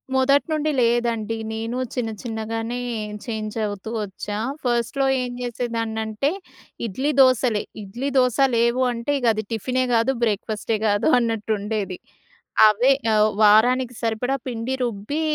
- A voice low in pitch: No, high, 230 Hz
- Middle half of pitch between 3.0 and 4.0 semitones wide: No, narrow, 2.5 semitones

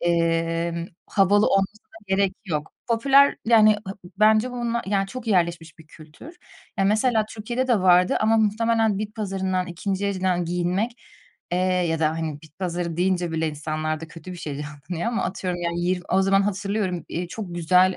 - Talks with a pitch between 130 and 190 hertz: Yes, medium, 185 Hz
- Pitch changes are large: No, average, 3.9 semitones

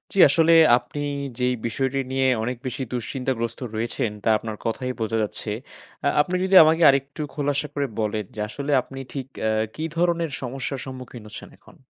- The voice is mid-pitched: No, low, 130 Hz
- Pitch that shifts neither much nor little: Yes, average, 3.8 semitones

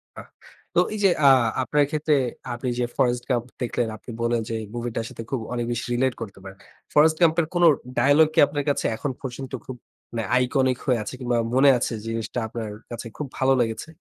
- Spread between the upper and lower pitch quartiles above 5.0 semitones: No, average, 3.4 semitones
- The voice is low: Yes, low, 125 Hz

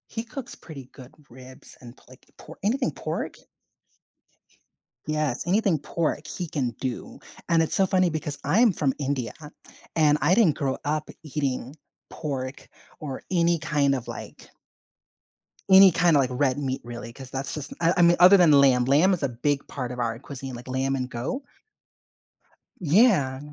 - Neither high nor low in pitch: Yes, medium, 145 Hz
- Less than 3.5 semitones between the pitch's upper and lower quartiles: No, average, 4.5 semitones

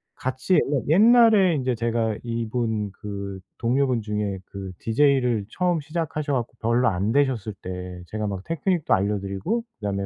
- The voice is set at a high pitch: No, low, 115 Hz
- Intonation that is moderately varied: No, wide, 5.9 semitones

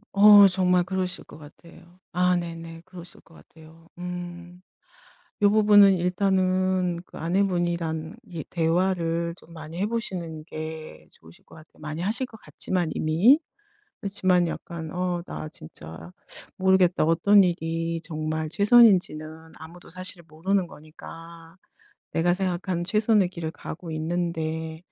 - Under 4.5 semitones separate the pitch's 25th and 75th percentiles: Yes, narrow, 2.5 semitones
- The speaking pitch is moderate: Yes, medium, 175 Hz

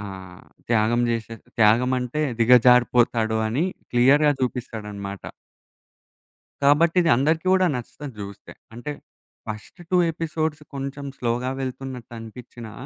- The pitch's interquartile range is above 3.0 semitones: Yes, average, 3.9 semitones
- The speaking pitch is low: Yes, low, 125 Hz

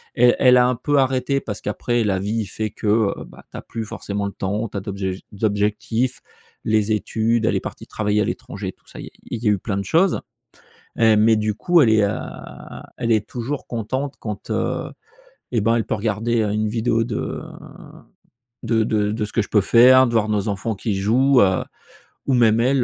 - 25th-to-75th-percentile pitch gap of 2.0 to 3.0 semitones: Yes, narrow, 2.5 semitones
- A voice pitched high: No, low, 110 Hz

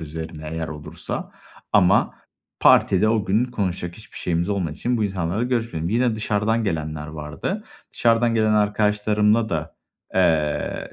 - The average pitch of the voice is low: Yes, low, 100 Hz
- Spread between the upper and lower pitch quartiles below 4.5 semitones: No, average, 5.2 semitones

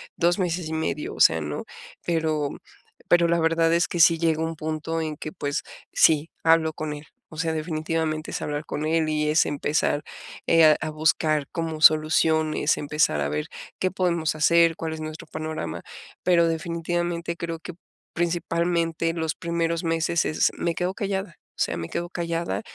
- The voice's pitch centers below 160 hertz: No, medium, 165 Hz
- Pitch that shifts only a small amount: Yes, narrow, 1.4 semitones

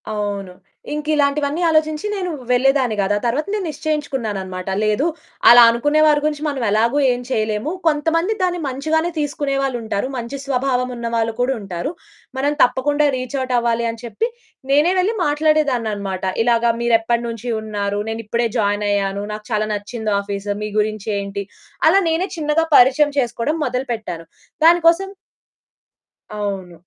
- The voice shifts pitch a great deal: Yes, wide, 5.7 semitones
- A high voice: Yes, high, 245 Hz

